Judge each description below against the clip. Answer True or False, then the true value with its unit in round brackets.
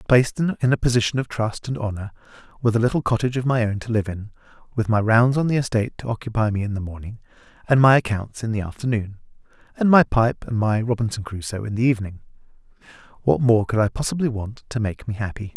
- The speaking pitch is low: True (115 Hz)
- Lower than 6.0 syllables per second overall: False (6.4 syllables/s)